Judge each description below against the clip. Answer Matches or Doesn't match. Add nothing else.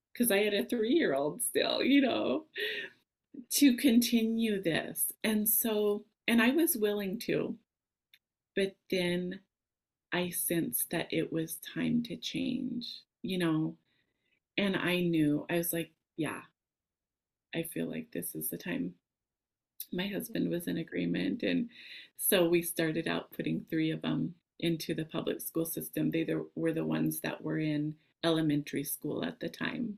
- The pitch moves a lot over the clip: Matches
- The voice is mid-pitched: Matches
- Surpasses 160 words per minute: Doesn't match